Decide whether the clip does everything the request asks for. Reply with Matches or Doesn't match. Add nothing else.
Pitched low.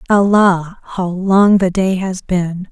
Doesn't match